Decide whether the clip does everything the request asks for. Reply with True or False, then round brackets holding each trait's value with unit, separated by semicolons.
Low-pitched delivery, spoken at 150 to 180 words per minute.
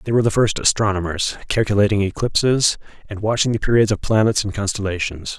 True (105 Hz; 165 wpm)